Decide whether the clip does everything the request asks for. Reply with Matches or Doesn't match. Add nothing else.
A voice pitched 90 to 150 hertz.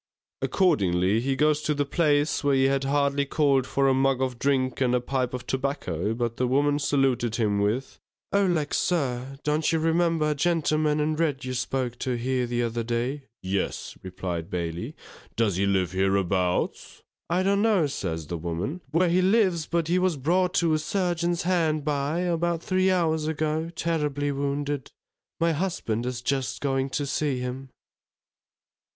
Matches